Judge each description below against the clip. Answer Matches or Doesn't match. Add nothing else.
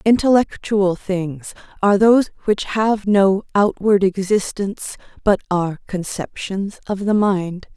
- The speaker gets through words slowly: Matches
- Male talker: Doesn't match